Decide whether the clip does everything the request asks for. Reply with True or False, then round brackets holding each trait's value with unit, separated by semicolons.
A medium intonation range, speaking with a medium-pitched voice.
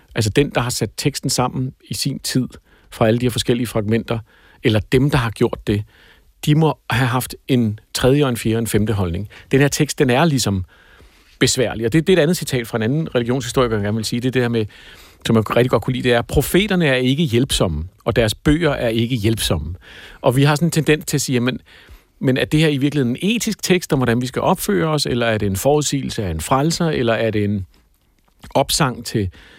False (4.6 semitones; 125 Hz)